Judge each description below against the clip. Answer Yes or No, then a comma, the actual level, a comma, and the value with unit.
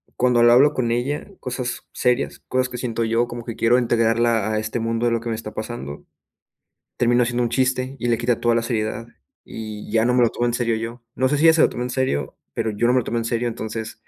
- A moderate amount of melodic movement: No, narrow, 1.5 semitones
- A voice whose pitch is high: No, low, 120 Hz